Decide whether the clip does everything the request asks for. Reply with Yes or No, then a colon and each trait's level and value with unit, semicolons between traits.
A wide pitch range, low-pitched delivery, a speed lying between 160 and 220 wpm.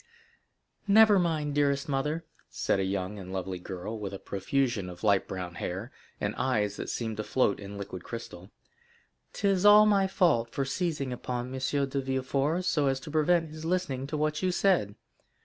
Yes: wide, 7.7 semitones; low, 130 Hz; average, 180 wpm